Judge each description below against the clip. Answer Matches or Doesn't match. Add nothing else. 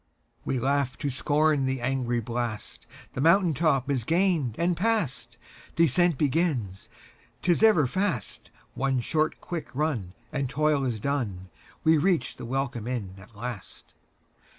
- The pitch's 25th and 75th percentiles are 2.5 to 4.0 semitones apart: Doesn't match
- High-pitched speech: Doesn't match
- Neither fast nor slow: Doesn't match